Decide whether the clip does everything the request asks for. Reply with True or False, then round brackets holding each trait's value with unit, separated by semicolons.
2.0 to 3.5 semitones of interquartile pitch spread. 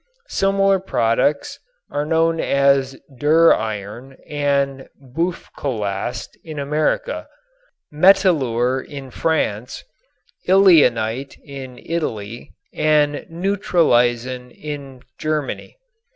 False (4.7 semitones)